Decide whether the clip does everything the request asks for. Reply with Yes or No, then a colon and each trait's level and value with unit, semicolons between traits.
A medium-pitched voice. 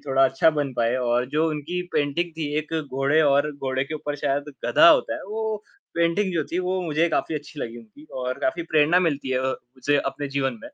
Yes: medium, 145 Hz